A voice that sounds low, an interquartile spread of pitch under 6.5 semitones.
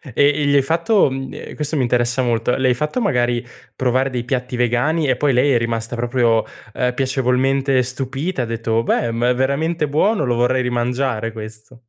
Yes: low, 125 Hz; narrow, 2.5 semitones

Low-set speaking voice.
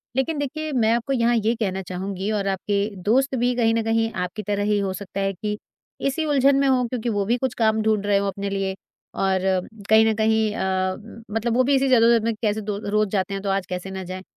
No: high, 215 Hz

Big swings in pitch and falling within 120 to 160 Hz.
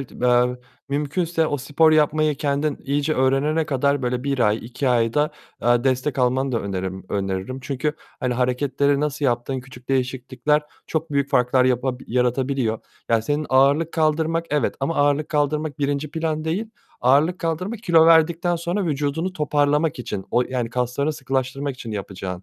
No: average, 3.5 semitones; medium, 140 Hz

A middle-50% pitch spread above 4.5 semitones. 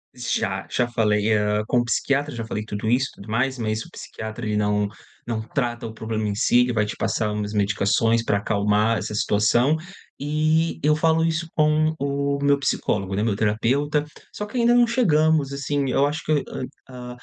Yes: wide, 5.5 semitones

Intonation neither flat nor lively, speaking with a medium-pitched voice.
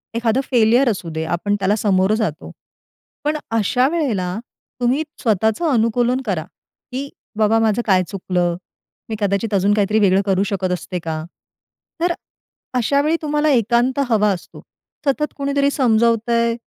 No: average, 4.5 semitones; high, 220 Hz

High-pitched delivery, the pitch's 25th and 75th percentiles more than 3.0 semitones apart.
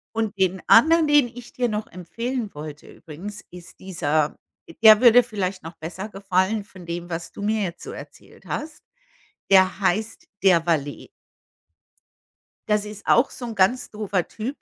Yes: high, 200 Hz; average, 4.1 semitones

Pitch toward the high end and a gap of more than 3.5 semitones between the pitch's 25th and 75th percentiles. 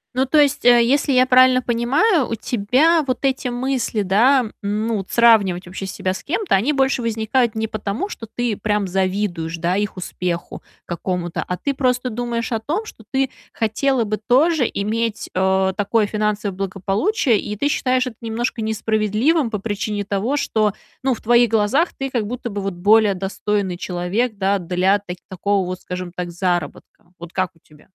Yes: high, 215 Hz; average, 4.6 semitones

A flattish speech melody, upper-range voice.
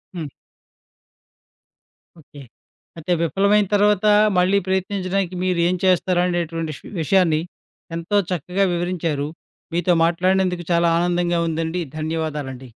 No: narrow, 2.2 semitones; medium, 175 Hz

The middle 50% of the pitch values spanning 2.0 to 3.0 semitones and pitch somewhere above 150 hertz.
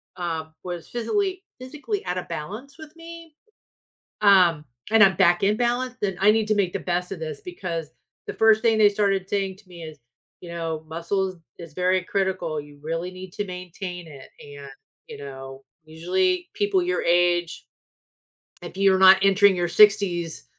No: average, 4.1 semitones; medium, 185 Hz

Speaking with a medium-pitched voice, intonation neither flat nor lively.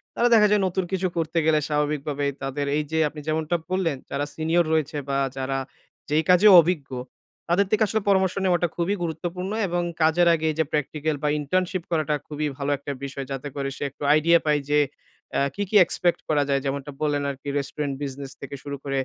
Yes: medium, 155 Hz; average, 3.4 semitones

